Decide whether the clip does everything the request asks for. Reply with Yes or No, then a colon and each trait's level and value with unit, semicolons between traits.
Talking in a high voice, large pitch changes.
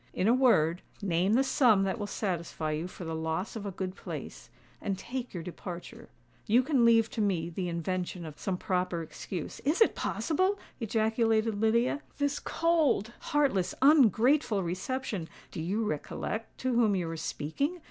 Yes: high, 205 Hz; wide, 5.8 semitones